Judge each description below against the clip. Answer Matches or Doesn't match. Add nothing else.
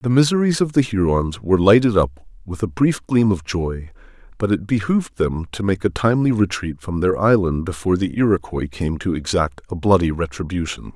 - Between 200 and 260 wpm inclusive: Doesn't match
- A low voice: Matches